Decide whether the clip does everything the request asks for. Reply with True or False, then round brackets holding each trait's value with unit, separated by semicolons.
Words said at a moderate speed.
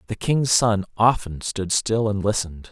True (175 wpm)